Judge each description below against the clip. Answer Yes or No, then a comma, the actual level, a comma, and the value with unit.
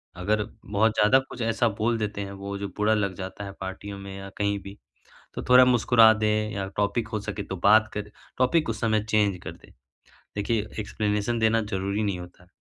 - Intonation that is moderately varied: No, narrow, 1.9 semitones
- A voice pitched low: Yes, low, 105 Hz